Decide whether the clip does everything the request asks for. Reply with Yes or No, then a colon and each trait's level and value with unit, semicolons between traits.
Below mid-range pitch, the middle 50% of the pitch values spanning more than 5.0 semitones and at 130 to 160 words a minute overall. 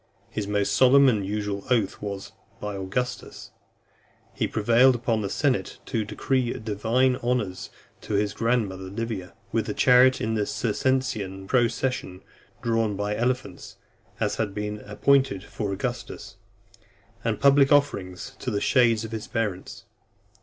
No: low, 110 Hz; average, 3.5 semitones; average, 140 wpm